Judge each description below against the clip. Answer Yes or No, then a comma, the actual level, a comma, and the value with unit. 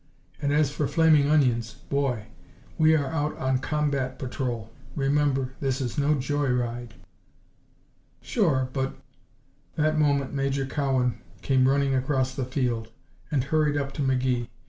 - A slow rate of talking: No, average, 145 wpm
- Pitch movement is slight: Yes, narrow, 2.3 semitones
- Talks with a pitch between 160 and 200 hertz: No, low, 135 Hz